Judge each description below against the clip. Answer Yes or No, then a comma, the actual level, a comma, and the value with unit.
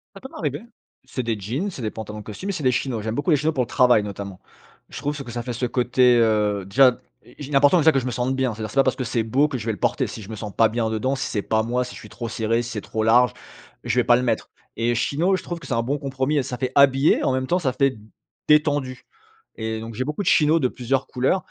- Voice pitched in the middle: No, low, 125 Hz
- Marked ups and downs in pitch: No, average, 3.7 semitones